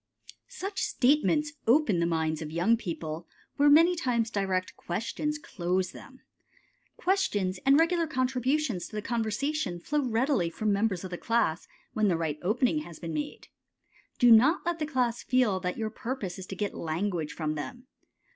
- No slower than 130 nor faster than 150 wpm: No, average, 165 wpm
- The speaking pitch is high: Yes, high, 220 Hz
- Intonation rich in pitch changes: Yes, wide, 7.8 semitones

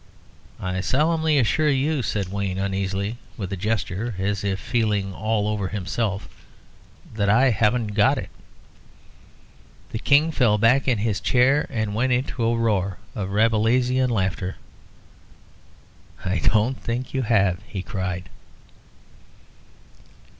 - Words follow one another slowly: Yes, slow, 125 wpm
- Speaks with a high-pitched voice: No, low, 105 Hz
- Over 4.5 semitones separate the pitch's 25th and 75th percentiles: No, average, 4.0 semitones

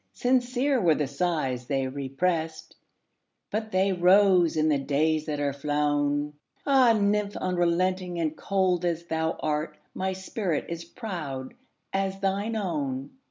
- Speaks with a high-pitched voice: No, medium, 170 Hz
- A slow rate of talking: Yes, slow, 120 wpm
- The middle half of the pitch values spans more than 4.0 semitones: Yes, average, 4.7 semitones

